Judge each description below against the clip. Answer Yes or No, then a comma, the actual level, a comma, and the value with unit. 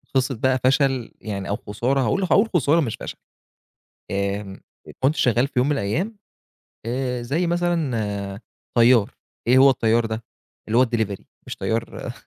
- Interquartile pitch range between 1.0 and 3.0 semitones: No, average, 3.8 semitones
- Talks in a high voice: No, low, 125 Hz